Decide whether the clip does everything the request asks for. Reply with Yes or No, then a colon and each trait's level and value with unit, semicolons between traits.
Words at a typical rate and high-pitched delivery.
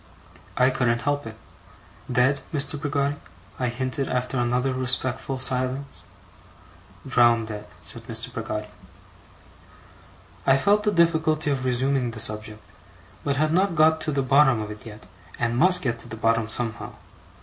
No: average, 150 wpm; low, 130 Hz